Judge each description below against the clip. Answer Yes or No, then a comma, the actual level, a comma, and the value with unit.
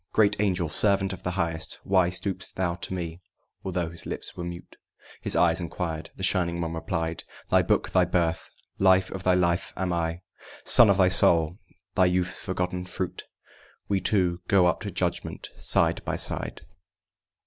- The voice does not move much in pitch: Yes, narrow, 1.7 semitones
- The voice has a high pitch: No, very low, 90 Hz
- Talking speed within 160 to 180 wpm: Yes, average, 170 wpm